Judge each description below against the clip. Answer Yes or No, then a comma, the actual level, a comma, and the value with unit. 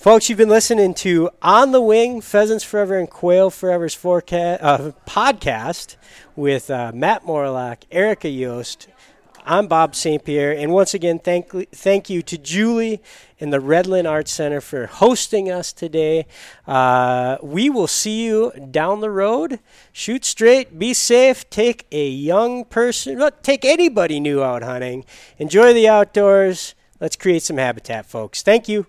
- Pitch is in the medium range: Yes, medium, 180 Hz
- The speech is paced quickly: No, average, 155 wpm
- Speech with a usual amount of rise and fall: No, wide, 6.9 semitones